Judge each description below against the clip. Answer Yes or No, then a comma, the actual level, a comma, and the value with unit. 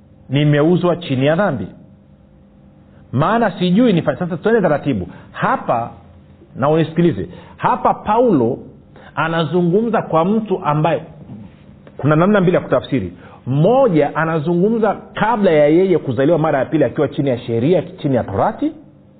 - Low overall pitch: No, medium, 155 Hz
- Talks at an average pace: Yes, average, 120 wpm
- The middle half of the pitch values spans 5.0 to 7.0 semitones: Yes, wide, 5.4 semitones